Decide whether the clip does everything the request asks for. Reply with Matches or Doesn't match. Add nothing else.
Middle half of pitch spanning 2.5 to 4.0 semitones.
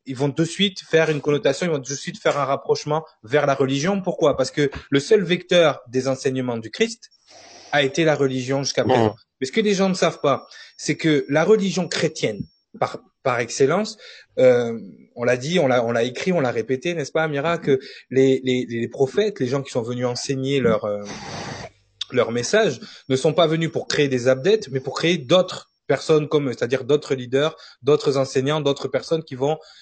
Doesn't match